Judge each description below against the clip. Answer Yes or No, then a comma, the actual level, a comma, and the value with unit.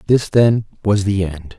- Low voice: Yes, low, 100 Hz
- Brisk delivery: No, average, 190 wpm